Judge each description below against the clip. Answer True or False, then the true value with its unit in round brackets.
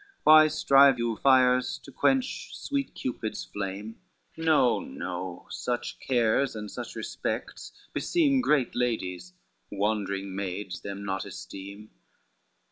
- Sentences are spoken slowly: True (115 wpm)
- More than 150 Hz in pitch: False (115 Hz)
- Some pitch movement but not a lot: False (5.7 semitones)